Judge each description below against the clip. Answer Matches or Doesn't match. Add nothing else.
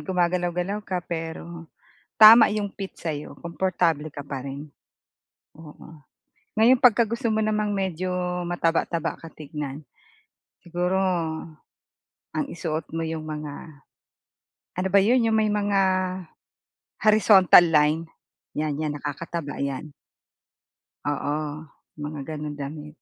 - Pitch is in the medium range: Matches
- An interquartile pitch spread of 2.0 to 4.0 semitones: Doesn't match